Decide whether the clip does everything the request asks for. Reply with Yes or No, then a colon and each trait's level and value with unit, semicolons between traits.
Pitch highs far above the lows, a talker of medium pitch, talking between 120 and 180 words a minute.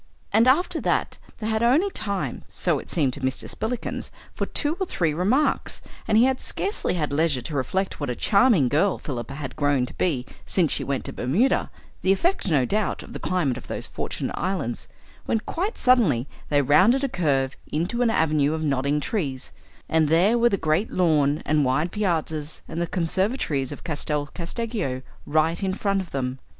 No: wide, 6.9 semitones; medium, 165 Hz; average, 190 wpm